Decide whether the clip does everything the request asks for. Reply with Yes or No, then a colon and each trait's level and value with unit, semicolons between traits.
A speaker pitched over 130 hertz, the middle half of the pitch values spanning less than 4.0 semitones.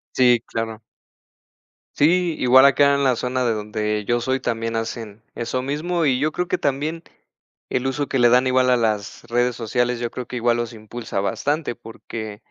No: low, 120 Hz; average, 2.8 semitones